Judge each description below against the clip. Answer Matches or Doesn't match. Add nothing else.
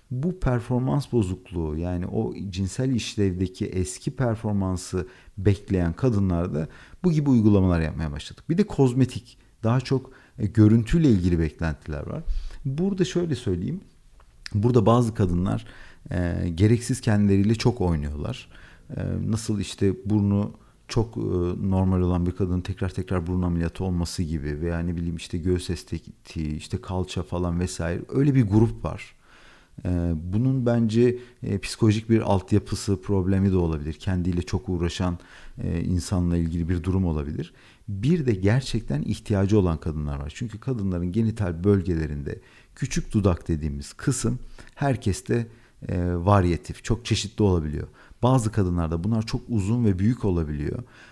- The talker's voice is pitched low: Matches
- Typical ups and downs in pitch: Matches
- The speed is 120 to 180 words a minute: Matches